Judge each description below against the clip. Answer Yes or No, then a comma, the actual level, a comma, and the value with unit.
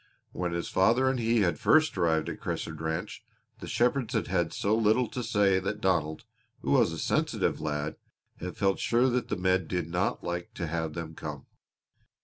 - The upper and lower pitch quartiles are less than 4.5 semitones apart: No, wide, 5.5 semitones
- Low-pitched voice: Yes, very low, 95 Hz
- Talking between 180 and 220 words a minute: Yes, average, 190 wpm